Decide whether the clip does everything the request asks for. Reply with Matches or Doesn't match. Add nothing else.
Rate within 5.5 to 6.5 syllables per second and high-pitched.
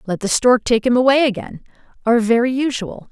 Matches